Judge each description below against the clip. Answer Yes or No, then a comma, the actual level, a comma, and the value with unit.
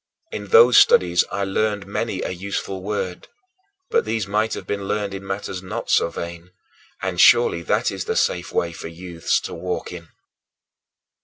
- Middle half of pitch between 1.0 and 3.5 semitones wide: Yes, average, 2.8 semitones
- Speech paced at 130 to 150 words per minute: No, average, 170 wpm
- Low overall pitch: Yes, very low, 95 Hz